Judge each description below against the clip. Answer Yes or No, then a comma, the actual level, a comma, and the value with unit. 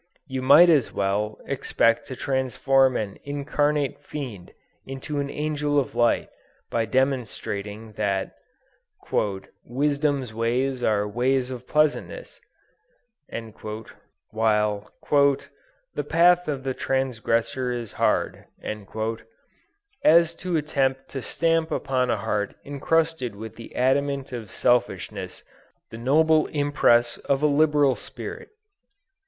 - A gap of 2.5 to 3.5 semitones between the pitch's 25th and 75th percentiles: No, average, 4.1 semitones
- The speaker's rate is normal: No, slow, 110 wpm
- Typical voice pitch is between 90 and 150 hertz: Yes, low, 135 Hz